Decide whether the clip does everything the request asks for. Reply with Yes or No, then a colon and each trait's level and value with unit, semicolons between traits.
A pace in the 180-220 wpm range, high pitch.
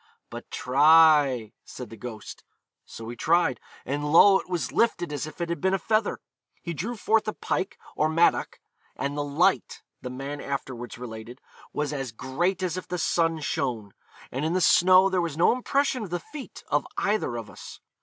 No: average, 190 wpm; medium, 155 Hz